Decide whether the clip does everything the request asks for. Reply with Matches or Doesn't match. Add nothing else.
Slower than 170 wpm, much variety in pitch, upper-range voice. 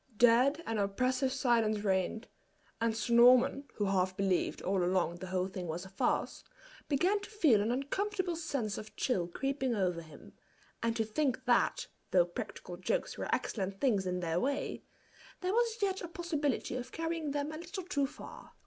Doesn't match